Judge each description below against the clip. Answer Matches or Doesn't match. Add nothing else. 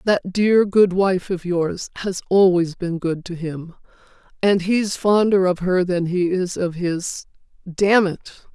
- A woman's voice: Matches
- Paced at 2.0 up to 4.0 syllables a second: Matches